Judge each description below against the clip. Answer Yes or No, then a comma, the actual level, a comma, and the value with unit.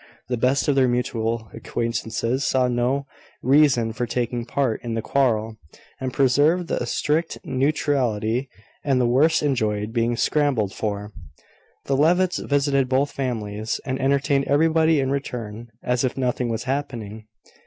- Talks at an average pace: Yes, average, 145 wpm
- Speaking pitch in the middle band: No, low, 125 Hz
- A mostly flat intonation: No, average, 3.4 semitones